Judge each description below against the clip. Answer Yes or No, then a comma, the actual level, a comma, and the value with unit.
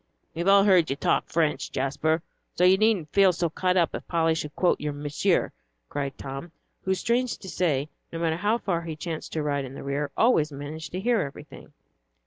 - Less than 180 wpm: No, fast, 205 wpm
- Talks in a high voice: No, medium, 165 Hz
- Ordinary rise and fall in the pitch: Yes, average, 4.0 semitones